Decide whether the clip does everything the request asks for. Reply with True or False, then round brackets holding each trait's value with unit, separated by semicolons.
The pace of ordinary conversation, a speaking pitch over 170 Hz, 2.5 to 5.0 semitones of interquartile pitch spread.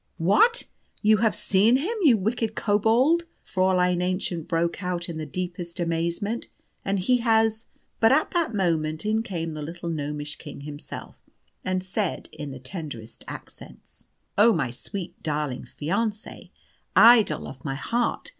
False (150 wpm; 185 Hz; 5.5 semitones)